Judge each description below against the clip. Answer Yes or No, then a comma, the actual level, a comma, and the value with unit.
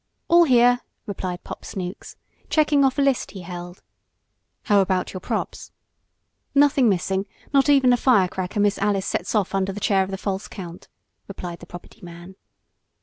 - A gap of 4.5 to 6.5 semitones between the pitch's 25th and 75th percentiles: Yes, average, 5.1 semitones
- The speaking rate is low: No, average, 165 wpm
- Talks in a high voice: Yes, high, 195 Hz